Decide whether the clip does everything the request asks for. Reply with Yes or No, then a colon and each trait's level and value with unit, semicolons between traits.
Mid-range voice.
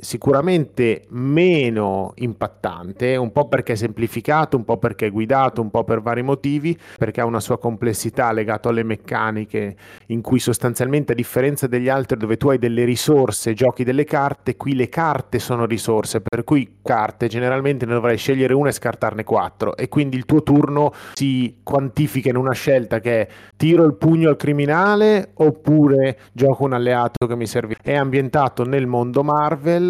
No: low, 125 Hz